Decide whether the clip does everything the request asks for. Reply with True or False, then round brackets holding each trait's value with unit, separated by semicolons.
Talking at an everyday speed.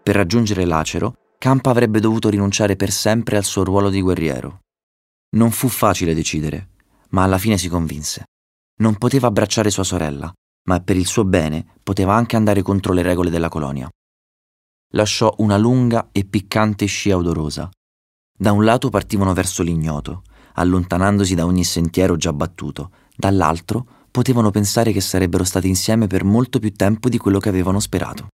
True (160 wpm)